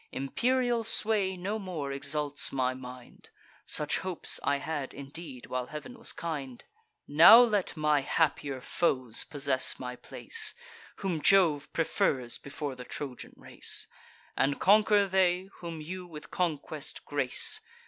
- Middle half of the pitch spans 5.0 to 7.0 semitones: Yes, average, 5.3 semitones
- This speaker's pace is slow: Yes, slow, 130 wpm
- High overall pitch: No, medium, 150 Hz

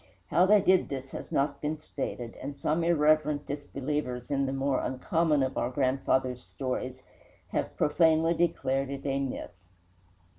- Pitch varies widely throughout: No, average, 2.8 semitones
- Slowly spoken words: No, average, 150 wpm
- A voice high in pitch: No, medium, 140 Hz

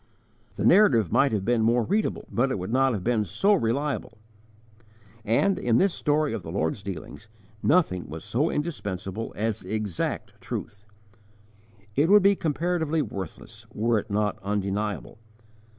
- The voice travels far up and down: Yes, wide, 6.7 semitones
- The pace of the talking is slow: No, average, 150 wpm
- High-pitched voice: No, low, 115 Hz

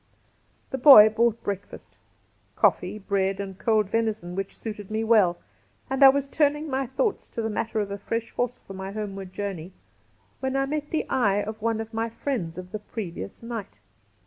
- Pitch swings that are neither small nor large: Yes, average, 3.7 semitones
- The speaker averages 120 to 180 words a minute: No, average, 195 wpm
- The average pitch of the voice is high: Yes, high, 215 Hz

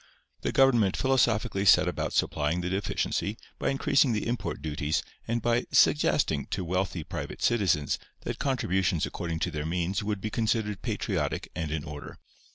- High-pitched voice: No, very low, 95 Hz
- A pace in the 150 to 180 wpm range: Yes, average, 160 wpm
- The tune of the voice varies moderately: No, wide, 6.2 semitones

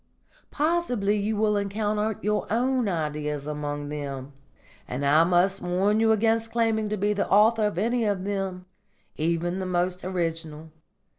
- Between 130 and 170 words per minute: Yes, average, 150 wpm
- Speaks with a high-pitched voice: Yes, high, 195 Hz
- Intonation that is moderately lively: Yes, average, 4.7 semitones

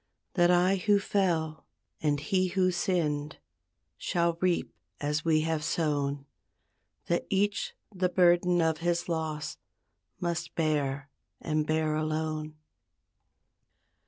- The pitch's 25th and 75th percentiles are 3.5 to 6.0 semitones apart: No, narrow, 2.6 semitones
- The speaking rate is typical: No, slow, 110 wpm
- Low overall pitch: No, medium, 160 Hz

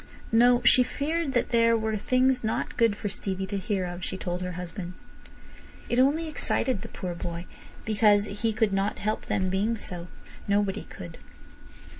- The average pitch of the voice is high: Yes, high, 205 Hz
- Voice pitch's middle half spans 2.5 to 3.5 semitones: No, average, 4.0 semitones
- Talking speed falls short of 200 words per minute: Yes, average, 170 wpm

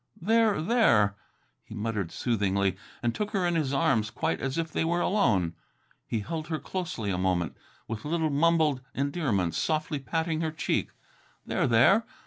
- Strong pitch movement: Yes, wide, 7.7 semitones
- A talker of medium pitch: Yes, medium, 145 Hz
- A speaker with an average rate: Yes, average, 160 wpm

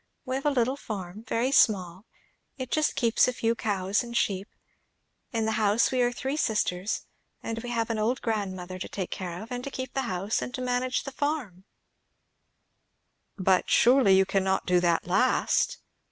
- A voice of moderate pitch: No, high, 225 Hz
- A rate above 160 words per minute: Yes, average, 180 wpm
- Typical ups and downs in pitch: Yes, average, 4.8 semitones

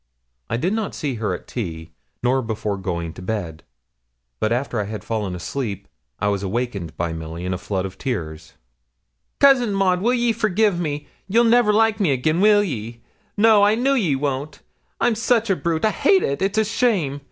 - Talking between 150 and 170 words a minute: No, average, 190 wpm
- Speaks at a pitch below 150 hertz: Yes, medium, 140 Hz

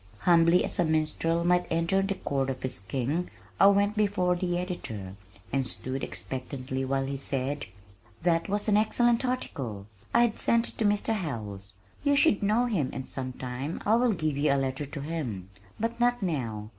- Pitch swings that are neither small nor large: No, wide, 7.3 semitones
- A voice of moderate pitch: Yes, medium, 165 Hz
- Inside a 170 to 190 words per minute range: Yes, average, 180 wpm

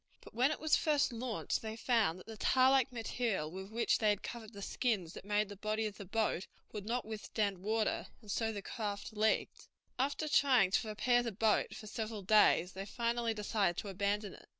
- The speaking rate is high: Yes, fast, 210 wpm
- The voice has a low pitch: No, high, 220 Hz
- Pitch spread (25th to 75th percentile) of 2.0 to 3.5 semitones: Yes, average, 2.7 semitones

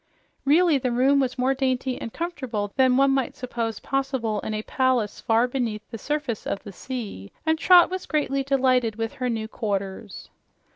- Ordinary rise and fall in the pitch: Yes, average, 3.4 semitones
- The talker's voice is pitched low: No, very high, 255 Hz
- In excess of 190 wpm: No, average, 180 wpm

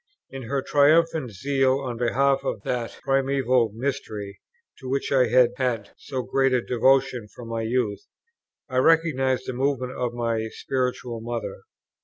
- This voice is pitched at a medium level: No, low, 130 Hz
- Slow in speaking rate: No, average, 150 wpm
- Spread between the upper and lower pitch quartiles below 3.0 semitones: Yes, narrow, 2.4 semitones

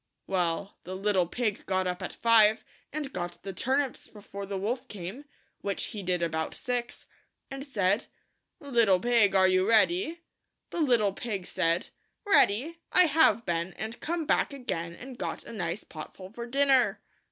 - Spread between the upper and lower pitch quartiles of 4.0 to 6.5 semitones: Yes, wide, 5.5 semitones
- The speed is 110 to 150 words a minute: No, average, 175 wpm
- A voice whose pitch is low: No, high, 210 Hz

